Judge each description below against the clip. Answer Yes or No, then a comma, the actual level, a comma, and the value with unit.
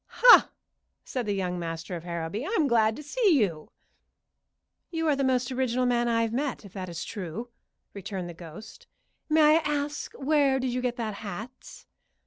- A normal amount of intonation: No, wide, 6.5 semitones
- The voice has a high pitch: Yes, high, 235 Hz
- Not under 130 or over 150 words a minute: No, average, 175 wpm